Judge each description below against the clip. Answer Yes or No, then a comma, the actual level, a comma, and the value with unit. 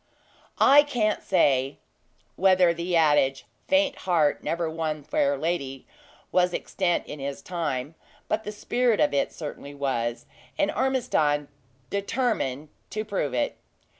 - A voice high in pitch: No, medium, 170 Hz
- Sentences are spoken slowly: Yes, slow, 130 wpm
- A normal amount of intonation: No, wide, 6.8 semitones